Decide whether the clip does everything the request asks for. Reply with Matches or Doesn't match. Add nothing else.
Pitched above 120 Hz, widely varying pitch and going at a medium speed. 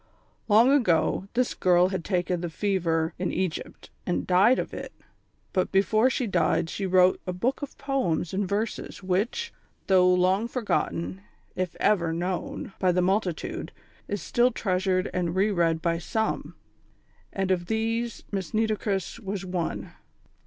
Doesn't match